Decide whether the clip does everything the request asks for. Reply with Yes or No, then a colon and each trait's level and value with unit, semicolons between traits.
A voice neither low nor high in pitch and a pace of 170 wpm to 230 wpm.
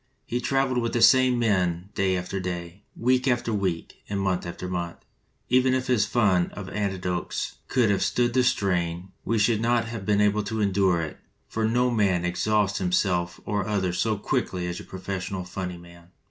No: low, 100 Hz; average, 190 wpm